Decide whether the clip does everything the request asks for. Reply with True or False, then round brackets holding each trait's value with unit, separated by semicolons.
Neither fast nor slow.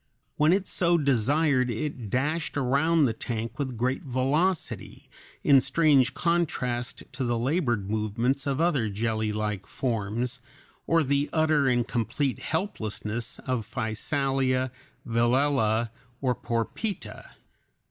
False (115 wpm)